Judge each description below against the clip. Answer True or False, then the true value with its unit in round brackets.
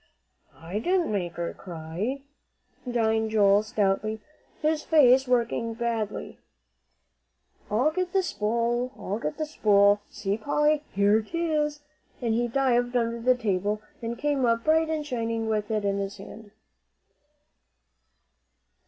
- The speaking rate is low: True (130 wpm)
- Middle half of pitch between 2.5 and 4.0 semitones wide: False (4.5 semitones)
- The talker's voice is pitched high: True (230 Hz)